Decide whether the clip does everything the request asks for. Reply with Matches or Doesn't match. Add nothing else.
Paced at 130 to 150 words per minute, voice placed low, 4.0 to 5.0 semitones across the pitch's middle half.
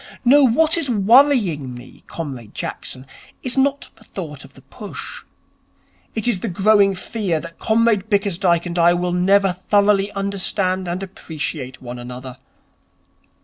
Doesn't match